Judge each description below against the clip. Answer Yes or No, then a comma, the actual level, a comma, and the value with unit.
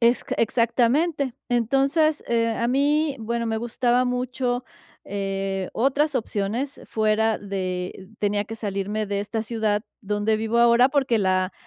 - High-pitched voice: Yes, high, 230 Hz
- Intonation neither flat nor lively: Yes, average, 3.4 semitones